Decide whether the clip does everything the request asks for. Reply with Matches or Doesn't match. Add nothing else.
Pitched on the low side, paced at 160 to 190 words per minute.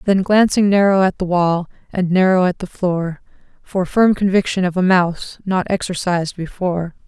Doesn't match